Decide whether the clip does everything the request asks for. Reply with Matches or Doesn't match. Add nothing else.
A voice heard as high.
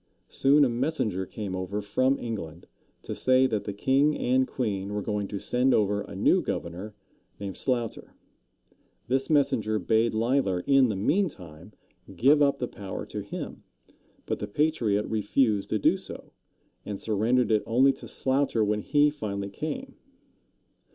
Doesn't match